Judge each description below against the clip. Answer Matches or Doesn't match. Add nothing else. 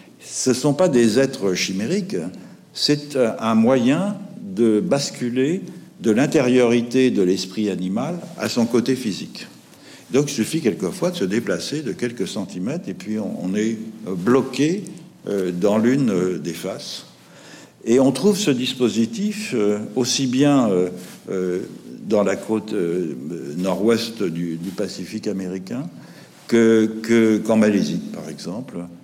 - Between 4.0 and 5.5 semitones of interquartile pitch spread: Matches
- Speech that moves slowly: Matches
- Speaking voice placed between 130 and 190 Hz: Doesn't match